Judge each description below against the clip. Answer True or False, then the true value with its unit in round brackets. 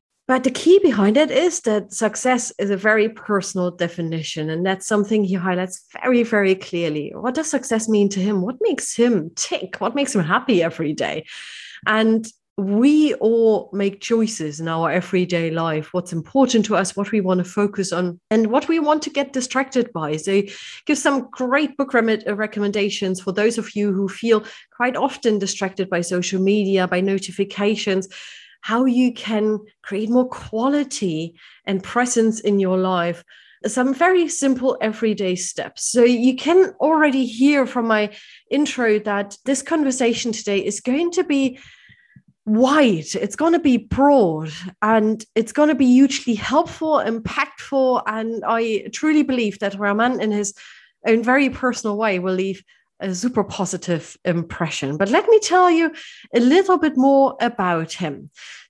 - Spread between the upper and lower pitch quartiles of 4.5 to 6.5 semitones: True (5.1 semitones)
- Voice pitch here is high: True (220 Hz)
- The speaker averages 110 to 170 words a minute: True (165 wpm)